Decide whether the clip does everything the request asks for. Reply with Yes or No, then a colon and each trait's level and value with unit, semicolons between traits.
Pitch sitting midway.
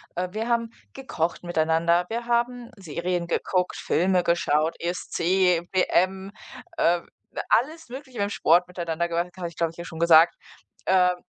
Yes: medium, 180 Hz